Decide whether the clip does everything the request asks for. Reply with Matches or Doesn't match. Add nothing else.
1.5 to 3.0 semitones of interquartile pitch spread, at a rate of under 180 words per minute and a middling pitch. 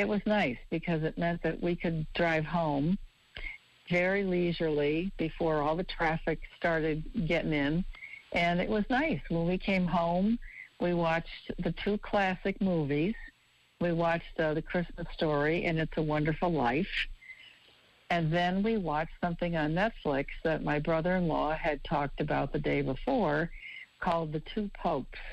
Matches